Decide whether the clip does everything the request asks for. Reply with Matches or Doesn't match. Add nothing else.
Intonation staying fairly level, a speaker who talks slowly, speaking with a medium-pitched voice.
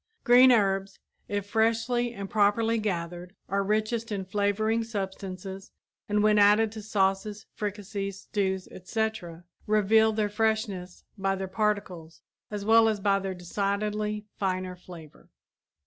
Doesn't match